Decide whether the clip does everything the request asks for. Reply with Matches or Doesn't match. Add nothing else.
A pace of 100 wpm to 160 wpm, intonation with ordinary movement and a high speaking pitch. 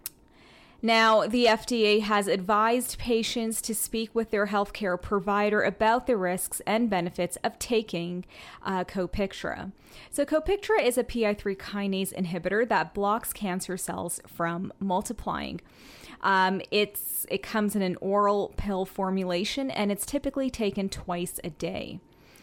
Matches